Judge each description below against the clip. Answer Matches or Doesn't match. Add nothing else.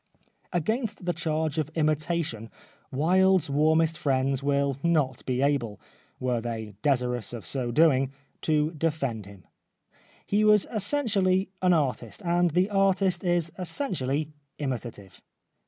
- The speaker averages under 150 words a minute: Matches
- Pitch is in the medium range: Matches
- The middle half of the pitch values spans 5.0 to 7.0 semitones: Matches